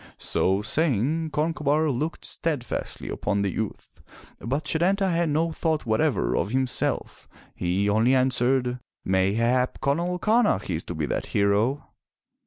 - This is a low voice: Yes, low, 130 Hz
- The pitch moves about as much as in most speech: No, wide, 7.2 semitones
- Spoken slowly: Yes, slow, 130 wpm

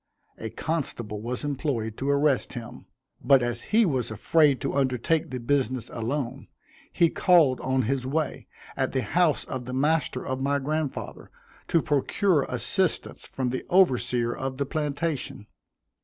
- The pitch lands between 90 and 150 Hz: Yes, low, 135 Hz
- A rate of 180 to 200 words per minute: No, average, 150 wpm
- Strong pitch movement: No, average, 3.3 semitones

